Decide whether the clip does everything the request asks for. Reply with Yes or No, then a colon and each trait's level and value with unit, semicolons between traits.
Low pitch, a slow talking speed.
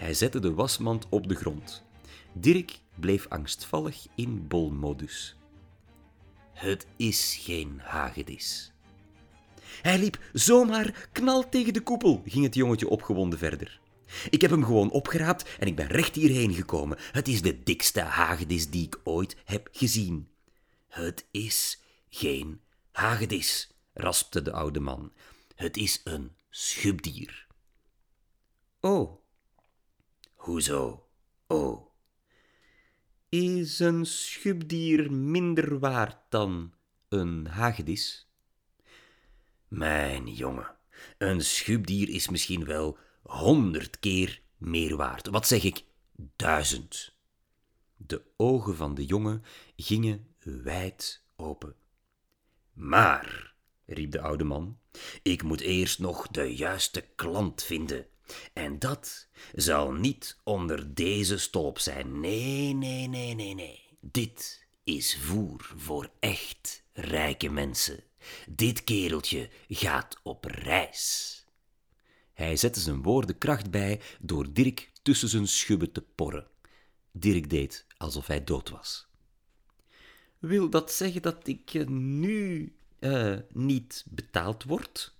Yes: low, 100 Hz; slow, 115 wpm